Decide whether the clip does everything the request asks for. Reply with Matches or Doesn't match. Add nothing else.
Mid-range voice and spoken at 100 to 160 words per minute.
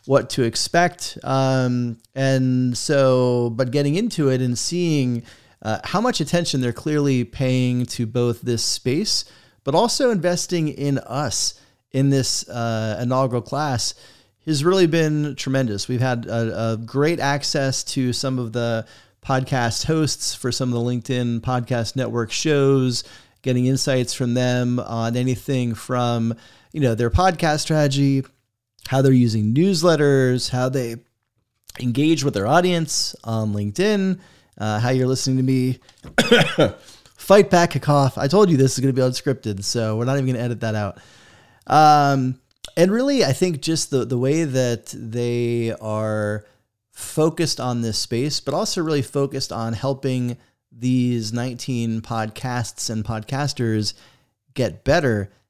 Doesn't match